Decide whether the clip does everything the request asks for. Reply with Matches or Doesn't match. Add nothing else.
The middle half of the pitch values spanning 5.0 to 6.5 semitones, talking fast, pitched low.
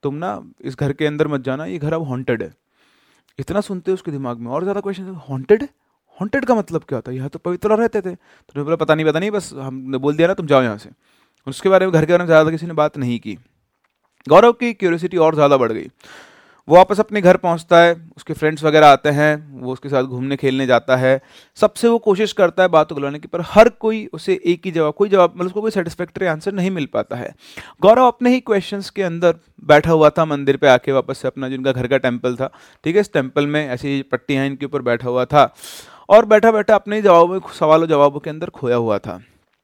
Doesn't match